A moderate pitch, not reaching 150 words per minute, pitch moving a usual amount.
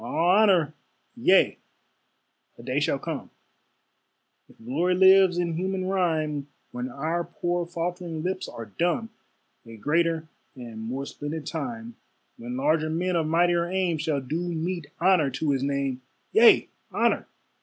Yes: medium, 165 Hz; average, 140 wpm; average, 4.1 semitones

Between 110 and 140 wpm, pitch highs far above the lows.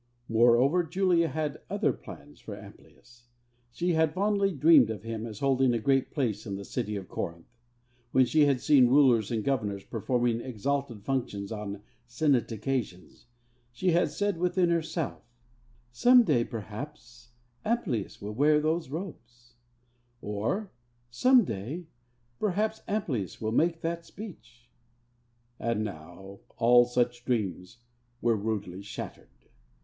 Yes: slow, 135 wpm; wide, 6.6 semitones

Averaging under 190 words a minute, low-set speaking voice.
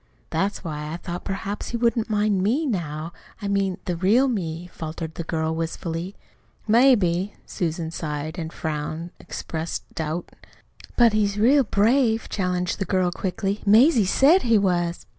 No: average, 150 wpm; medium, 185 Hz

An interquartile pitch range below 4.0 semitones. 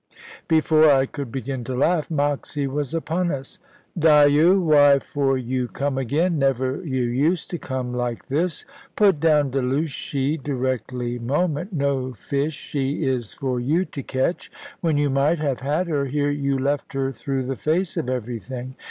Yes: average, 2.8 semitones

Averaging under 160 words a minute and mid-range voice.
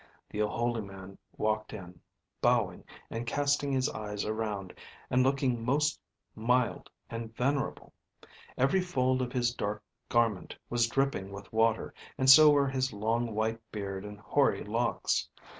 No: average, 140 wpm; low, 115 Hz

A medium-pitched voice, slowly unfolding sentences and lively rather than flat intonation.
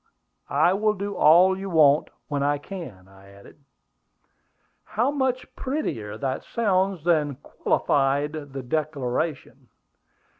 Yes: medium, 155 Hz; slow, 115 wpm; wide, 5.9 semitones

